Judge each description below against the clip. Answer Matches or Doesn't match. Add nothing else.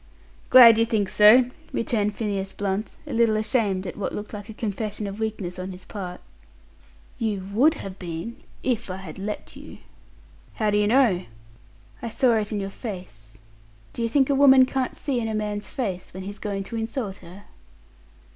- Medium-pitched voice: Doesn't match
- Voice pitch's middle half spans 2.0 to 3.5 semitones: Matches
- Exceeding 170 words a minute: Matches